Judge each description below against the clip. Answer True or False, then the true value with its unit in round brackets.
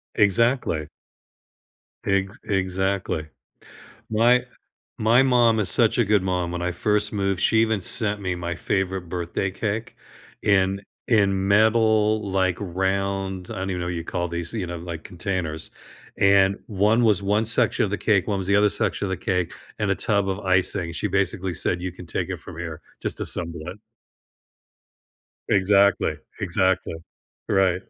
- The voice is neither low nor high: False (95 Hz)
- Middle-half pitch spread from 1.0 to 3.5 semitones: True (2.5 semitones)